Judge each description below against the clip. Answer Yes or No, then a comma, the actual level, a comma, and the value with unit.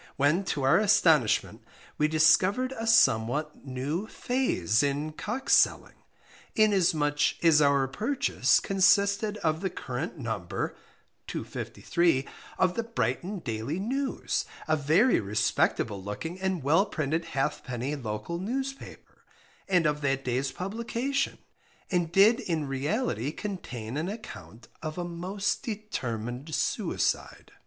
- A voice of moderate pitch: Yes, medium, 160 Hz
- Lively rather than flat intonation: Yes, wide, 6.7 semitones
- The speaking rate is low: Yes, slow, 120 wpm